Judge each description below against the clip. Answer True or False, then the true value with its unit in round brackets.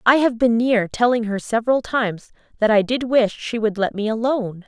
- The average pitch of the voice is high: True (225 Hz)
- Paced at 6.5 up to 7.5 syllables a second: False (5.4 syllables/s)